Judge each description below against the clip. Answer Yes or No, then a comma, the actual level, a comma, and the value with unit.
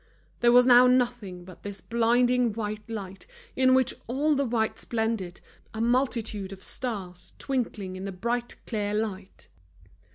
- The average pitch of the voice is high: Yes, high, 225 Hz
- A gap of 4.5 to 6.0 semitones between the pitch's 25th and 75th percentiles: No, average, 3.8 semitones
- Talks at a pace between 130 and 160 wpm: Yes, average, 150 wpm